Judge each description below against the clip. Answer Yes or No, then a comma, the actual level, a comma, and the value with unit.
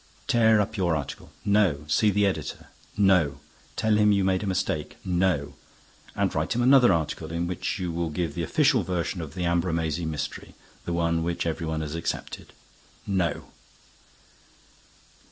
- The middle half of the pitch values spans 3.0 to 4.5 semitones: Yes, average, 3.5 semitones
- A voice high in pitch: No, very low, 85 Hz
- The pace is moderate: Yes, average, 160 wpm